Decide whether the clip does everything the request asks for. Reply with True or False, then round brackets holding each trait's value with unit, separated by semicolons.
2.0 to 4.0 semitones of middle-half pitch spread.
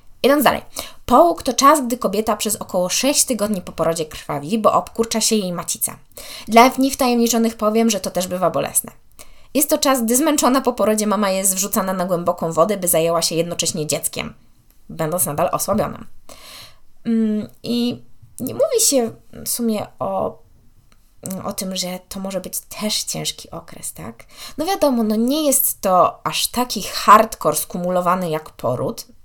False (5.1 semitones)